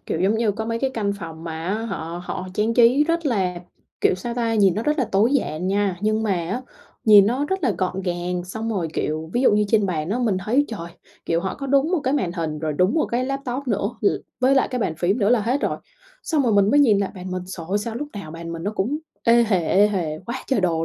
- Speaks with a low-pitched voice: No, high, 210 Hz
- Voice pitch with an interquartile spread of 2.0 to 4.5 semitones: No, average, 5.1 semitones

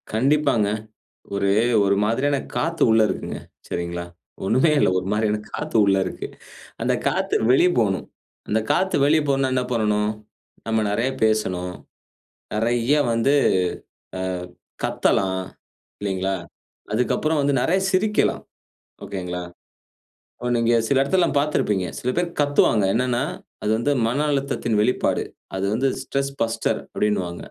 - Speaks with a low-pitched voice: Yes, low, 115 Hz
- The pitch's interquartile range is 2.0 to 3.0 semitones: No, average, 5.3 semitones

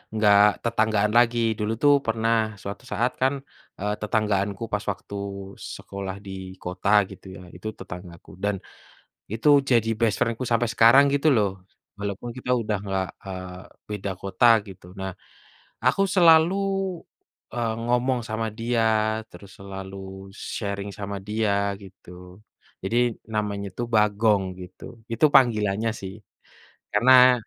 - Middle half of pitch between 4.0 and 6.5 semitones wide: No, average, 2.9 semitones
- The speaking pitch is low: Yes, low, 105 Hz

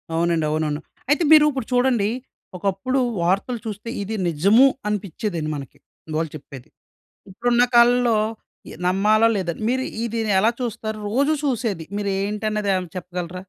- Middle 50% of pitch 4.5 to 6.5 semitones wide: Yes, average, 5.0 semitones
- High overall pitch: Yes, high, 210 Hz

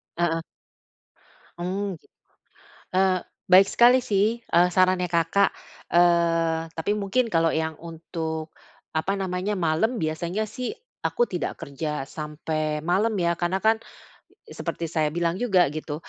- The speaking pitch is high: No, medium, 175 Hz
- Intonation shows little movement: No, average, 3.3 semitones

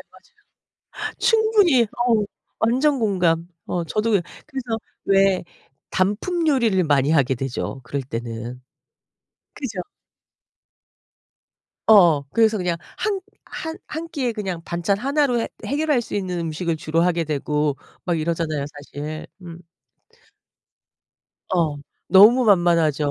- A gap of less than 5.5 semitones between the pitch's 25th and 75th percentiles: No, wide, 7.4 semitones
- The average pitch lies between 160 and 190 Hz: Yes, medium, 185 Hz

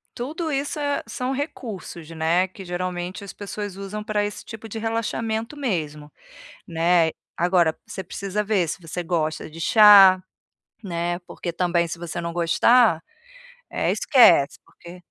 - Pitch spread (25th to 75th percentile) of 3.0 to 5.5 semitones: Yes, average, 4.5 semitones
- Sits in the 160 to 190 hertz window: Yes, medium, 185 Hz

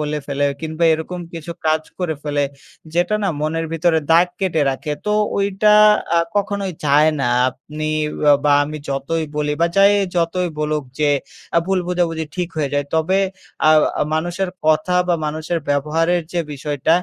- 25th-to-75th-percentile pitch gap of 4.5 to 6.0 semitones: No, average, 2.8 semitones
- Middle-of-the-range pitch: Yes, medium, 160 Hz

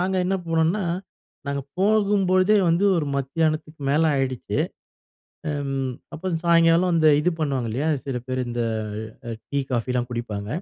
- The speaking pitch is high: No, medium, 155 Hz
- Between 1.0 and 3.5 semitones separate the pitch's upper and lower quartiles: No, wide, 5.4 semitones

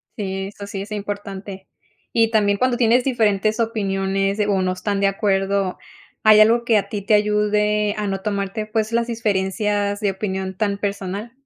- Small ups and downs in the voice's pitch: Yes, narrow, 1.7 semitones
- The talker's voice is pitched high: Yes, high, 205 Hz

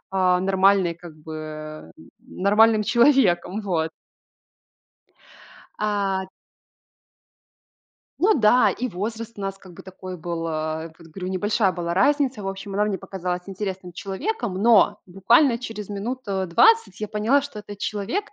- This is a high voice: Yes, high, 195 Hz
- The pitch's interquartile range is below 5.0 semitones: Yes, average, 3.6 semitones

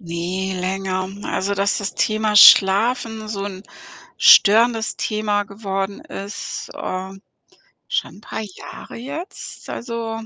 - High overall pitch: Yes, high, 200 Hz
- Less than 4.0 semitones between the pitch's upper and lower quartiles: Yes, narrow, 2.4 semitones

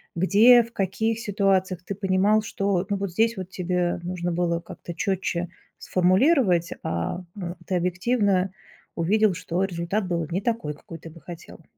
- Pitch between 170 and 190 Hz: Yes, medium, 185 Hz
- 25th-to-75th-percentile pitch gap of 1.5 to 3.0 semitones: Yes, average, 2.7 semitones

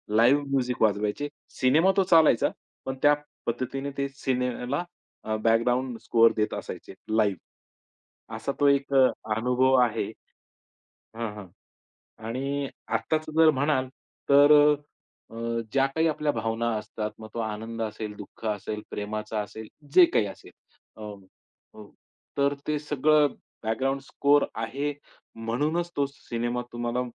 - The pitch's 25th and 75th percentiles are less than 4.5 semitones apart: Yes, average, 4.1 semitones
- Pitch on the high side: No, low, 125 Hz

